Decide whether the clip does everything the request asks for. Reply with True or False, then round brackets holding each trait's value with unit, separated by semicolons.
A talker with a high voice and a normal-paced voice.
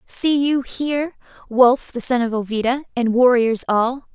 True (250 Hz; 160 wpm)